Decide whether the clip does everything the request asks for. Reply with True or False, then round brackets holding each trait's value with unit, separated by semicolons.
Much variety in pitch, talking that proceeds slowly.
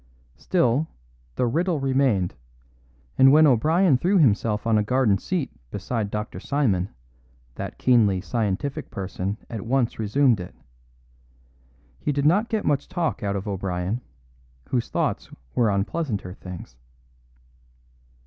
True (6.1 semitones; 130 wpm)